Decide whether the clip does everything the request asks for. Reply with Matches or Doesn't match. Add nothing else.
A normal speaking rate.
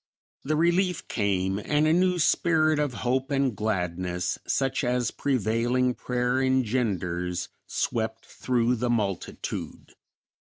Doesn't match